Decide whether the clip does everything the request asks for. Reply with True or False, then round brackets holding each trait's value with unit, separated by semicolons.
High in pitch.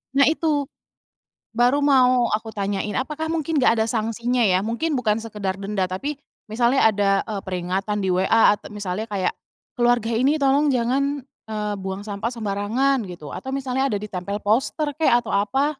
True (225 Hz)